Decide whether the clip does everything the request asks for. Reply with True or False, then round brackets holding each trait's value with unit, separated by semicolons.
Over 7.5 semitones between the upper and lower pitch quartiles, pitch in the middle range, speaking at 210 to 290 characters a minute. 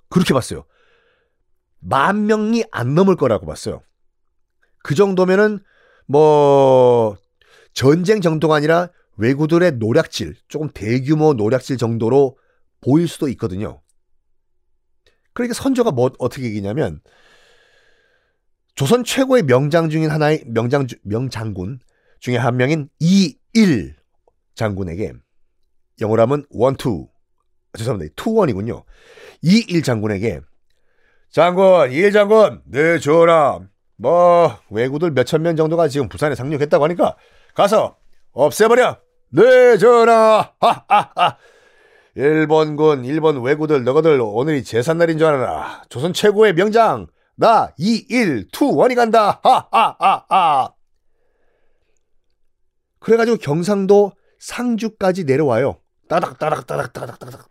True (9.0 semitones; 155 Hz; 255 characters per minute)